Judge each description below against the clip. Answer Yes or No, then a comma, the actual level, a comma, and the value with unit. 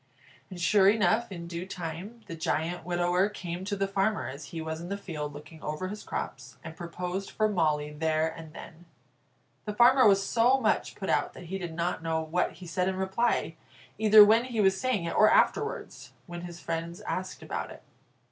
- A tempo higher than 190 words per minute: Yes, average, 200 wpm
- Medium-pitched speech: Yes, medium, 180 Hz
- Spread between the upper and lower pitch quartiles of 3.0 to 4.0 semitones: Yes, average, 3.6 semitones